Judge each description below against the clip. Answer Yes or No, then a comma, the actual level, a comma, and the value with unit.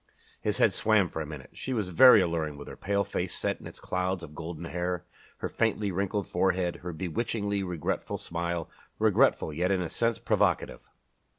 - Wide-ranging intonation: No, average, 3.1 semitones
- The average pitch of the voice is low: Yes, very low, 90 Hz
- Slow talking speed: No, average, 185 wpm